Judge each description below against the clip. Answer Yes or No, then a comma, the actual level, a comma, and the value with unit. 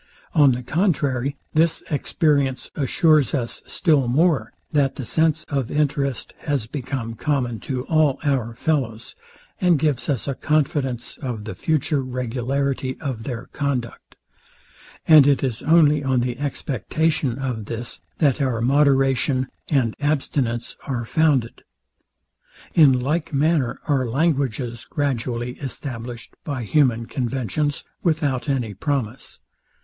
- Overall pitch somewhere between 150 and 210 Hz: No, low, 135 Hz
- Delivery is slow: Yes, slow, 125 wpm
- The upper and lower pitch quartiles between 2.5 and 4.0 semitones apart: Yes, average, 3.4 semitones